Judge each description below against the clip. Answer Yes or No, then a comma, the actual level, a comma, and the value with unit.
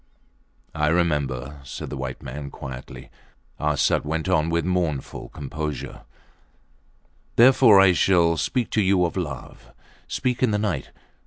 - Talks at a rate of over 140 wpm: No, slow, 135 wpm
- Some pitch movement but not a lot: Yes, average, 4.9 semitones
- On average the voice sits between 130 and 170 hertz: No, very low, 80 Hz